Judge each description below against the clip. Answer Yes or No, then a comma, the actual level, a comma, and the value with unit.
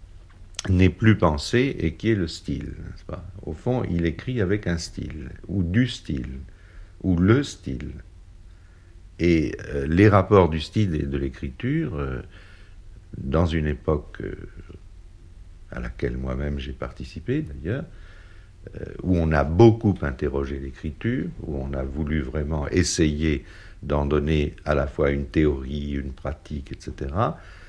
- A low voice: Yes, very low, 85 Hz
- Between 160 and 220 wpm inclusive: No, slow, 145 wpm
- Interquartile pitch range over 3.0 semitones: Yes, average, 4.1 semitones